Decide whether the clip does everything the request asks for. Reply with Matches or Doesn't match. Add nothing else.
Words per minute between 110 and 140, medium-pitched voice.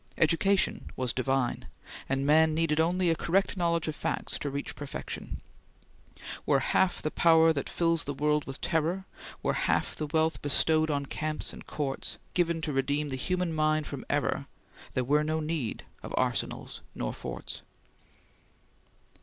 Doesn't match